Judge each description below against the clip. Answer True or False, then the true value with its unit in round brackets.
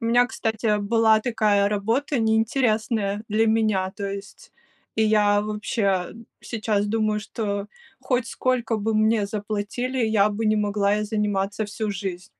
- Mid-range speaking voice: False (215 Hz)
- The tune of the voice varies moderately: False (1.6 semitones)